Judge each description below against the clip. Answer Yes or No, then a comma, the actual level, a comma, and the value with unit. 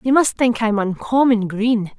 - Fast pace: No, average, 180 wpm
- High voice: Yes, high, 225 Hz